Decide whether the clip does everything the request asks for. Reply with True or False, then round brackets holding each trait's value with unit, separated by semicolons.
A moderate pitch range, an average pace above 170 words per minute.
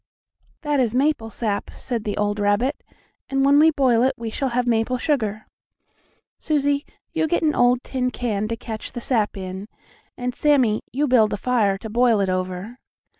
True (4.1 semitones; 180 wpm)